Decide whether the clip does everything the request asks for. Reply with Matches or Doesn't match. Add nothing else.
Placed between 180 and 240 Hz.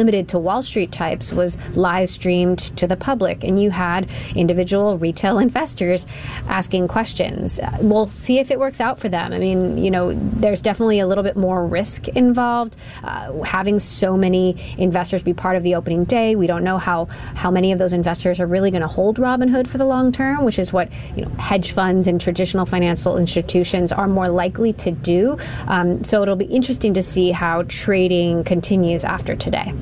Matches